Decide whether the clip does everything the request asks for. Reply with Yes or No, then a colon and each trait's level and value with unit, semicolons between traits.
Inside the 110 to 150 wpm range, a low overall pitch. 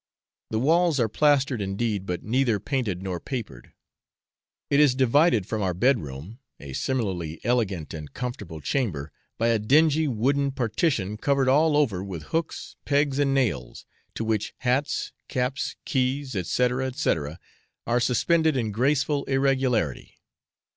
Yes: average, 140 wpm; low, 125 Hz